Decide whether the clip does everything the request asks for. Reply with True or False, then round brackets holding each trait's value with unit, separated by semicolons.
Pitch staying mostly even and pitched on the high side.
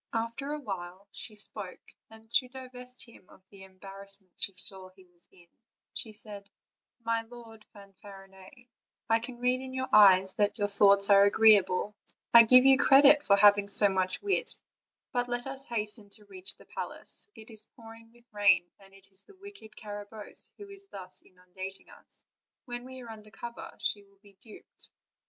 False (3.6 semitones; 210 Hz)